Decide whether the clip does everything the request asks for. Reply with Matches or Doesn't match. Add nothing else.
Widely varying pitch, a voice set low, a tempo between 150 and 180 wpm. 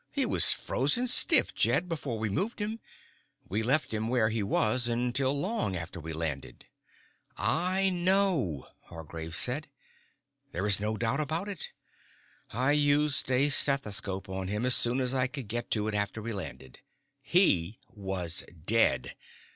Matches